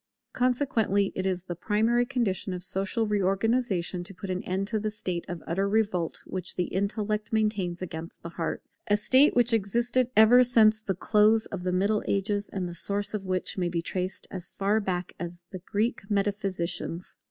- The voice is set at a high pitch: Yes, high, 200 Hz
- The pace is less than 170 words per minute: No, average, 185 wpm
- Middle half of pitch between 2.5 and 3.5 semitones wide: Yes, average, 3.0 semitones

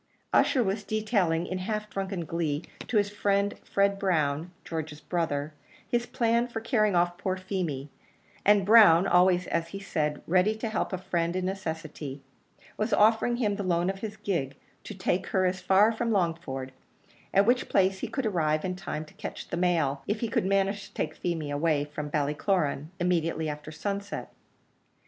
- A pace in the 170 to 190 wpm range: Yes, average, 175 wpm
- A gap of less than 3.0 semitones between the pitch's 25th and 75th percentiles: No, average, 4.2 semitones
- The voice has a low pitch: No, medium, 185 Hz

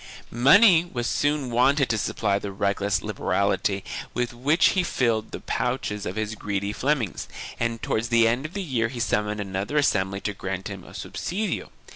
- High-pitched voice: No, low, 115 Hz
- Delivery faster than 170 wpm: Yes, average, 180 wpm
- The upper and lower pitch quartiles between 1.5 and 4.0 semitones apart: No, average, 5.0 semitones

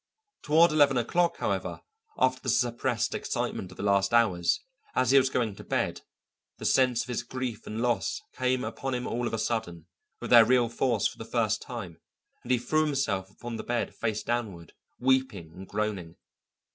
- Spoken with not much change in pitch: No, average, 3.8 semitones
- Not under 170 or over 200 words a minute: Yes, average, 185 wpm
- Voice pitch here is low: Yes, low, 120 Hz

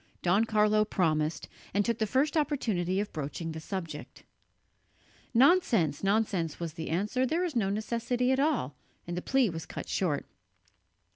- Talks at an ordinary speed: Yes, average, 155 wpm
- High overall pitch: Yes, high, 205 Hz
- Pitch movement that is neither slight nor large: No, wide, 6.7 semitones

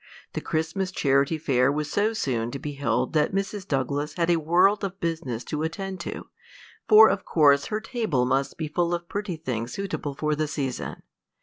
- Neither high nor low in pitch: Yes, medium, 155 Hz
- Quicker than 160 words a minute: Yes, average, 190 wpm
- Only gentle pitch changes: No, average, 5.1 semitones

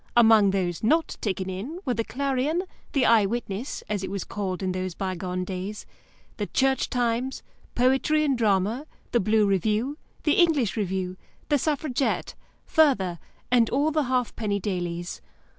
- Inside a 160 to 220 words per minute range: No, average, 150 wpm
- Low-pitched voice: No, high, 220 Hz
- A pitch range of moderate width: No, wide, 5.8 semitones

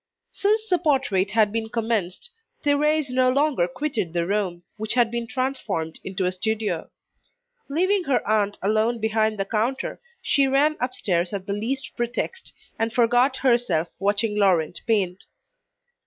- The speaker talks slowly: No, average, 145 wpm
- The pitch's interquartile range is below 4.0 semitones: No, average, 4.9 semitones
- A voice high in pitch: Yes, high, 225 Hz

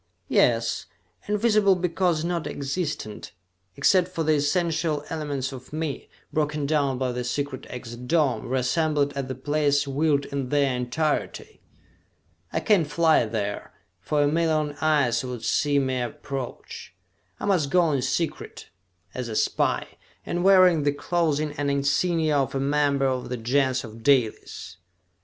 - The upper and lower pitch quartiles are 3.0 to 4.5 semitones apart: Yes, average, 3.4 semitones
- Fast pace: No, average, 145 wpm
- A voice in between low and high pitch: Yes, medium, 145 Hz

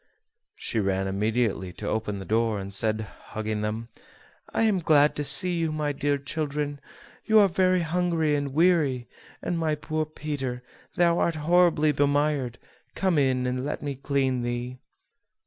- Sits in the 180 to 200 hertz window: No, medium, 145 Hz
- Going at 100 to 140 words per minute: No, average, 160 wpm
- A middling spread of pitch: Yes, average, 4.7 semitones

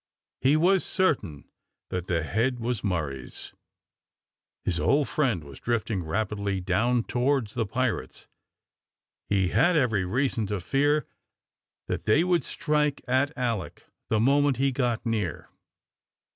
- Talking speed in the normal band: No, slow, 130 wpm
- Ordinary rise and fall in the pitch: No, wide, 6.0 semitones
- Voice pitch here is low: Yes, low, 115 Hz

